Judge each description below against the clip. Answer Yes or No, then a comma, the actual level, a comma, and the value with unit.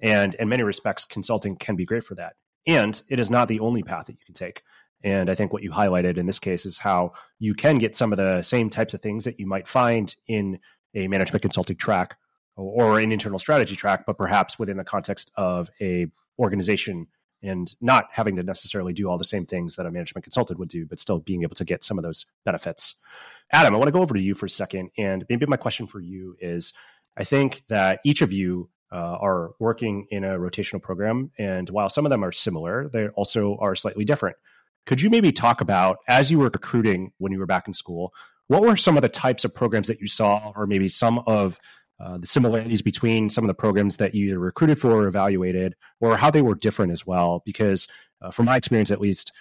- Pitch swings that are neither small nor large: Yes, average, 3.5 semitones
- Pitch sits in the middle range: No, low, 100 Hz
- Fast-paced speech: Yes, fast, 235 wpm